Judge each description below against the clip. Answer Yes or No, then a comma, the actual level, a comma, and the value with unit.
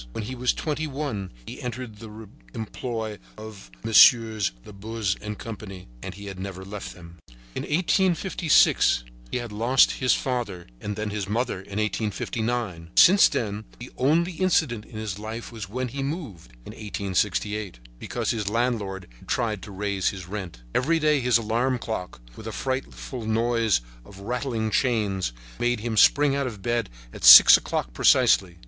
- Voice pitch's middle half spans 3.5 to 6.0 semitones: Yes, average, 3.8 semitones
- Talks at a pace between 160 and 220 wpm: Yes, average, 165 wpm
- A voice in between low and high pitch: No, low, 110 Hz